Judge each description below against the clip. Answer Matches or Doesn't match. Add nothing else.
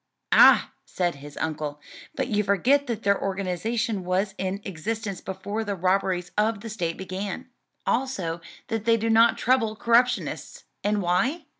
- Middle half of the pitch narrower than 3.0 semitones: Doesn't match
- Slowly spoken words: Doesn't match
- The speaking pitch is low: Doesn't match